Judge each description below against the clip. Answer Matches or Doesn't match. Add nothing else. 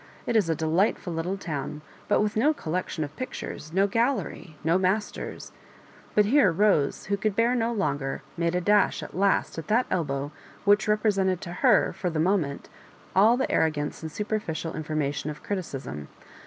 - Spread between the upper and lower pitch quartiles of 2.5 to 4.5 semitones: Doesn't match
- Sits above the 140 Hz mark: Matches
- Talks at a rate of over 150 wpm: Matches